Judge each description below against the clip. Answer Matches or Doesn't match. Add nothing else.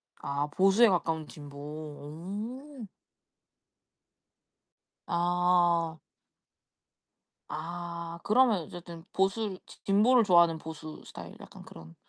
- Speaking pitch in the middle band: Matches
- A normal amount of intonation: Matches